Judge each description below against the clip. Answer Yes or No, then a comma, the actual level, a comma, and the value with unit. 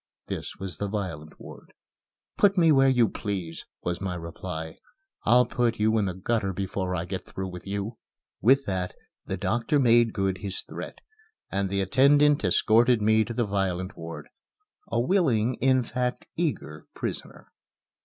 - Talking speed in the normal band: Yes, average, 160 wpm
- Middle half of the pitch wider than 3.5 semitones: Yes, average, 4.8 semitones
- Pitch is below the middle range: Yes, low, 105 Hz